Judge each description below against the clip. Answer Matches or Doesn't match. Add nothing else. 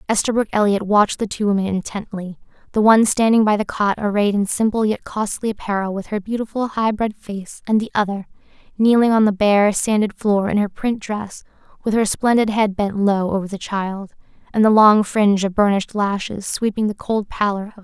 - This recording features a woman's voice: Matches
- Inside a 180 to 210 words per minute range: Matches